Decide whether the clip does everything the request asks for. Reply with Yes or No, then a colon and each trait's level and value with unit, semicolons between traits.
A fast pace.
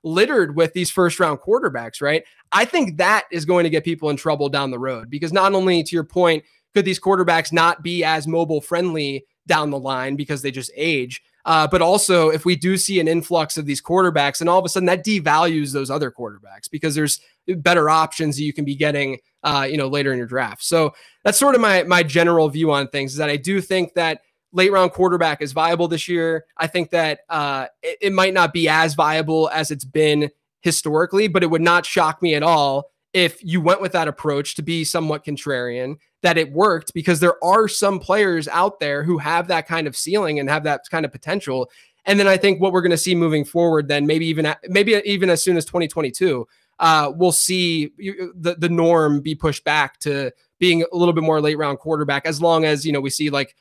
Yes: fast, 225 wpm